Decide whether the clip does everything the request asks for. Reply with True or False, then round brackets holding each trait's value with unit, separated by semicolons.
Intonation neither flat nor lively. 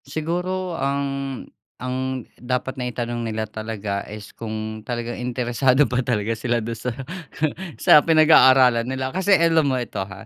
True (3.3 semitones)